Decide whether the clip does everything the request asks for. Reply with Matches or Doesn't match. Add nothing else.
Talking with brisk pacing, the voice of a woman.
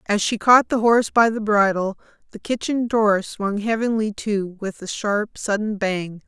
Doesn't match